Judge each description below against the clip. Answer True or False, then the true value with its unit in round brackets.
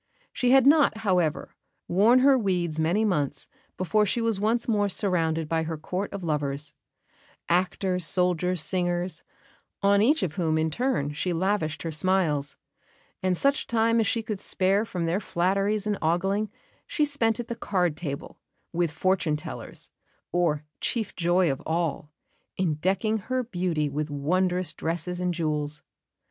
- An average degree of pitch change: True (4.6 semitones)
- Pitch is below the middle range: False (180 Hz)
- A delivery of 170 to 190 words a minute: False (155 wpm)